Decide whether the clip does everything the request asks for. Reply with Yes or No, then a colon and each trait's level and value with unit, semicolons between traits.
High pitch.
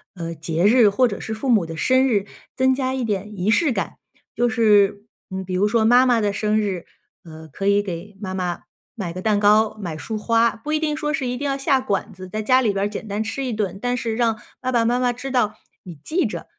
Yes: high, 215 Hz